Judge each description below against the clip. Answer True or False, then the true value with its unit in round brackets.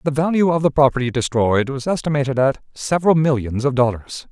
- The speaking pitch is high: False (140 Hz)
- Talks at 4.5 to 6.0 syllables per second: True (5.9 syllables/s)